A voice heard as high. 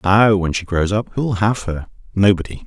No: low, 100 Hz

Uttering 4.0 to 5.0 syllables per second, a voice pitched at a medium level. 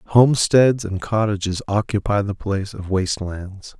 No: 4.6 syllables/s; low, 100 Hz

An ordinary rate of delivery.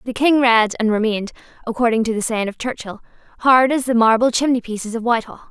Yes: average, 195 wpm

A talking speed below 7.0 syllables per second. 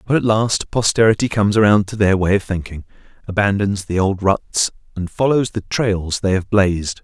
Yes: 5.1 syllables/s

